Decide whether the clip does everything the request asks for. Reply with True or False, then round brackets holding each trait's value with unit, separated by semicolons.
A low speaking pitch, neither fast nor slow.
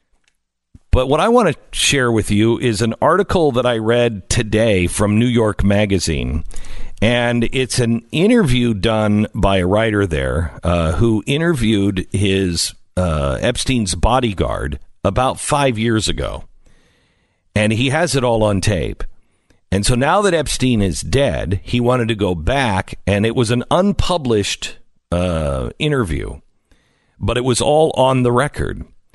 True (110 Hz; 150 wpm)